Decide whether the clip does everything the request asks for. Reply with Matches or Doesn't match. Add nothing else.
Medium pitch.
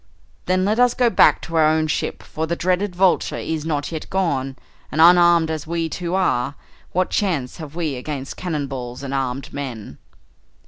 Matches